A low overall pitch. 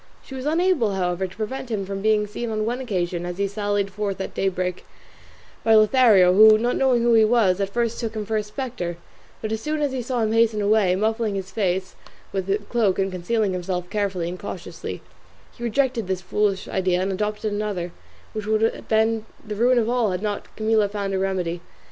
No: high, 210 Hz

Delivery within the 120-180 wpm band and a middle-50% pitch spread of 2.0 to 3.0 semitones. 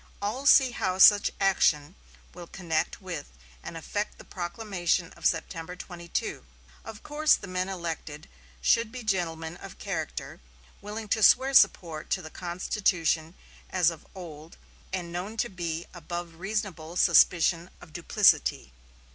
No: average, 140 wpm; average, 3.6 semitones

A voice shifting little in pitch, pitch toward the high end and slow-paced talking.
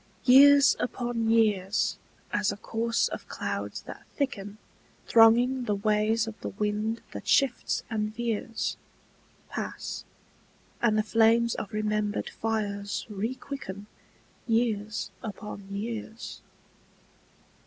Yes: narrow, 1.9 semitones; high, 220 Hz; slow, 105 wpm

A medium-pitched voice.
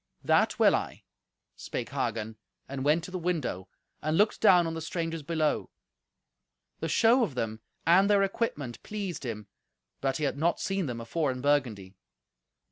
Yes: medium, 155 Hz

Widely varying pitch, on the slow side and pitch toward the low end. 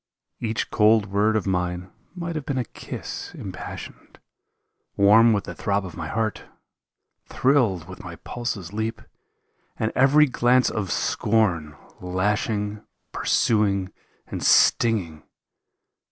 No: average, 3.5 semitones; slow, 125 wpm; low, 105 Hz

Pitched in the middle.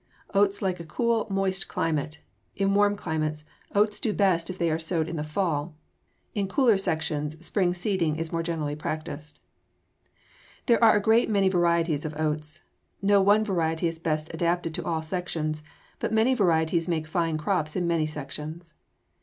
Yes: medium, 170 Hz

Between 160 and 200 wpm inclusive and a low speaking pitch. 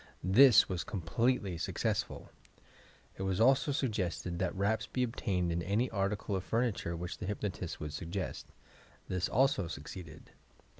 No: average, 150 wpm; very low, 95 Hz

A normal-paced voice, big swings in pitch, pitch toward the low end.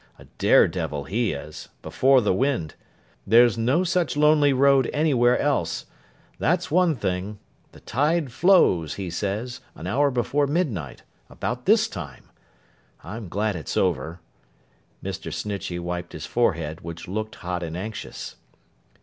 No: slow, 130 wpm; wide, 8.2 semitones; low, 110 Hz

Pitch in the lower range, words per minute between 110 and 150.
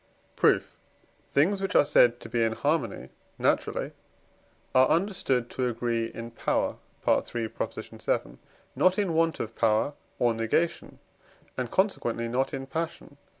Yes: low, 130 Hz; average, 140 wpm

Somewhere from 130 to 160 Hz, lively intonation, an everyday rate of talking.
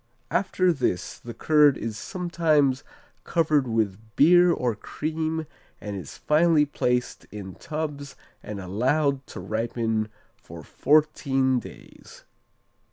No: medium, 140 Hz; wide, 5.7 semitones; slow, 110 wpm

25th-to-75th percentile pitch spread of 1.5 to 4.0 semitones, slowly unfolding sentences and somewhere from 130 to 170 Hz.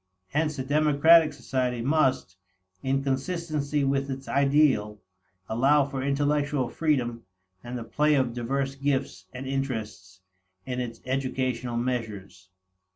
Yes: average, 2.9 semitones; slow, 120 wpm; low, 135 Hz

